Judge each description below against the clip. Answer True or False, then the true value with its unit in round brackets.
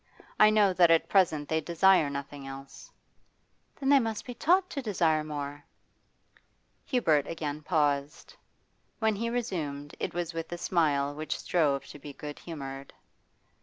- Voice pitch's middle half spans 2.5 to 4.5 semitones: False (5.1 semitones)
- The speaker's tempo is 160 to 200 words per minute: False (150 wpm)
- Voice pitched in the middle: True (160 Hz)